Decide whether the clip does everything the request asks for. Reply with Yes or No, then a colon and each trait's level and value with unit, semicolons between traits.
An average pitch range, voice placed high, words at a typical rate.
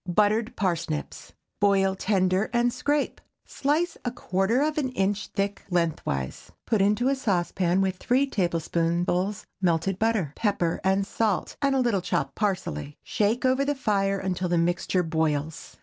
Yes: average, 4.6 semitones; high, 195 Hz; average, 150 wpm